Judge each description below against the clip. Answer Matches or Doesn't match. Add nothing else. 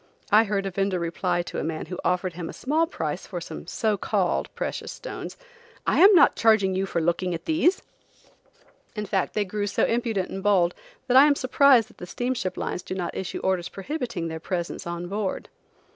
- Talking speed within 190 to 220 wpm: Matches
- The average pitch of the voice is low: Doesn't match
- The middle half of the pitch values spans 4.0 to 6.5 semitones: Matches